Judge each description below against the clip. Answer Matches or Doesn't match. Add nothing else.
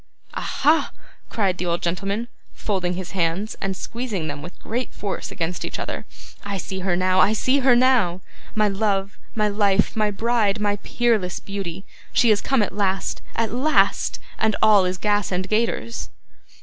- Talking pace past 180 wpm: Doesn't match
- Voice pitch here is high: Matches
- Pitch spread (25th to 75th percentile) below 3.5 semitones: Matches